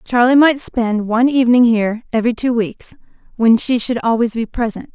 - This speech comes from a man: No, female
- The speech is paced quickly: No, average, 180 wpm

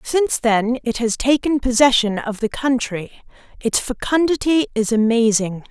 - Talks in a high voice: Yes, high, 245 Hz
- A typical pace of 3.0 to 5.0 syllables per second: Yes, 4.7 syllables/s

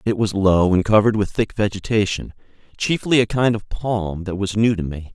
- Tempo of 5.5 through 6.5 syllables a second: No, 5.2 syllables/s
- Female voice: No, male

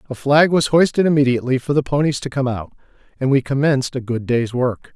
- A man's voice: Yes, male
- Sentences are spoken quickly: Yes, fast, 220 wpm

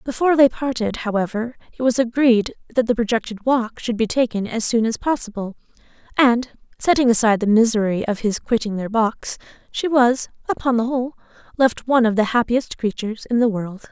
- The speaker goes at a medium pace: Yes, average, 180 wpm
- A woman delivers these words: Yes, female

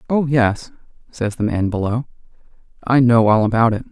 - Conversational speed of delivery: Yes, average, 170 wpm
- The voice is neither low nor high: No, low, 115 Hz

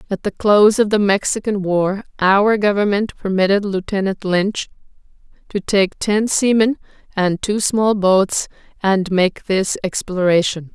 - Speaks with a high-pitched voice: Yes, high, 200 Hz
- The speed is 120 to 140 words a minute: Yes, slow, 135 wpm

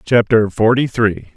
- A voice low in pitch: Yes, low, 110 Hz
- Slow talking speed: Yes, slow, 130 wpm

